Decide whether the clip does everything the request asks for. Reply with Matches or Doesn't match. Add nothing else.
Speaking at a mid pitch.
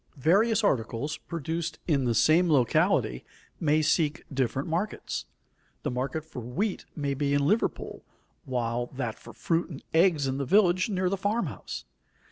Matches